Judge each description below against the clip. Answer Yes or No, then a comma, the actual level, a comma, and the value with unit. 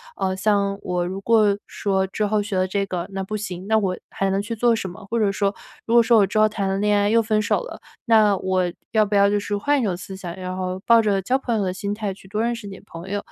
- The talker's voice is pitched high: Yes, high, 200 Hz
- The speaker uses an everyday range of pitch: No, narrow, 2.1 semitones